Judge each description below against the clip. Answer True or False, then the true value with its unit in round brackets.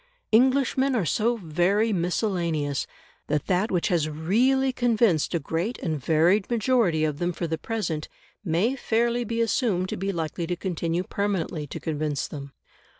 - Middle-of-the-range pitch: True (180 Hz)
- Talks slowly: False (155 wpm)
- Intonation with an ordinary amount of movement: False (6.1 semitones)